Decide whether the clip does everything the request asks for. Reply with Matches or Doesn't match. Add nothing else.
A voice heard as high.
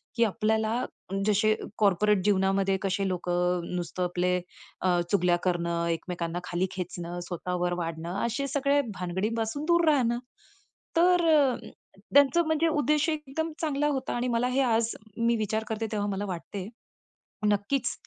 Matches